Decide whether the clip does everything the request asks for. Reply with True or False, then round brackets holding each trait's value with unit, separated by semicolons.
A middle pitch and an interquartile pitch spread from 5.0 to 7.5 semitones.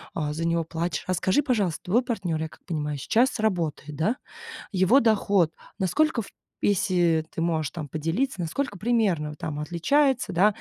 True (180 Hz; 5.5 semitones)